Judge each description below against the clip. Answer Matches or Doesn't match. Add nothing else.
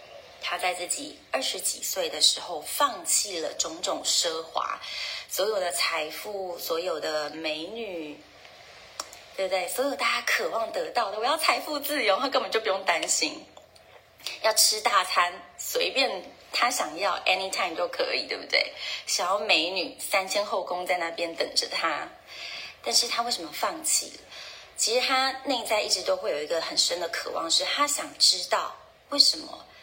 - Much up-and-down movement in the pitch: Matches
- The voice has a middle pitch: Doesn't match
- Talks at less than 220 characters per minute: Doesn't match